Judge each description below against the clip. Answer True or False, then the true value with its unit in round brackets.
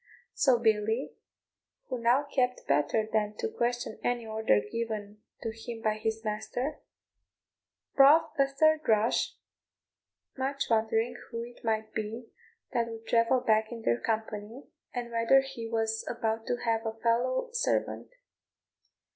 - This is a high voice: True (230 Hz)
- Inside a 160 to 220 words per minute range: False (140 wpm)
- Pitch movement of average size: False (1.9 semitones)